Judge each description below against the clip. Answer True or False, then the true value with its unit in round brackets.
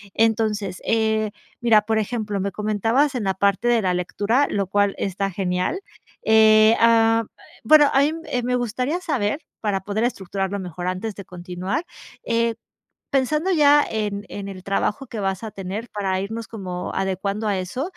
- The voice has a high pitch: True (210 Hz)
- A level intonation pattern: False (3.0 semitones)